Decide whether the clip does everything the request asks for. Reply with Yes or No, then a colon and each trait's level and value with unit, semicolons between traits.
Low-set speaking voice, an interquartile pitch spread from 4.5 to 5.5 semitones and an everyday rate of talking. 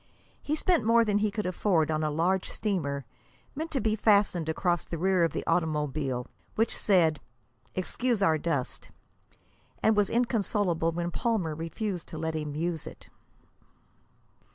No: medium, 175 Hz; average, 4.9 semitones; average, 155 wpm